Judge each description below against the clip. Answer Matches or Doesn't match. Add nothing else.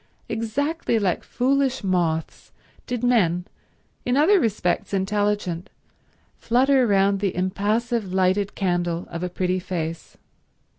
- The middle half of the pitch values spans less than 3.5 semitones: Doesn't match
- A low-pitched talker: Doesn't match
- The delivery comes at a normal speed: Doesn't match